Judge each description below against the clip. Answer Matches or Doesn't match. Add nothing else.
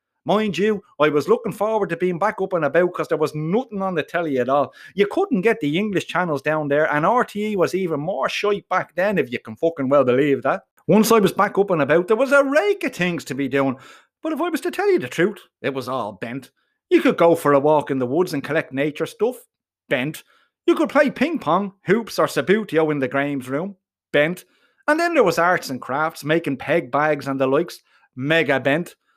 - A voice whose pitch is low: Doesn't match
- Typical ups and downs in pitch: Doesn't match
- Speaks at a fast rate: Matches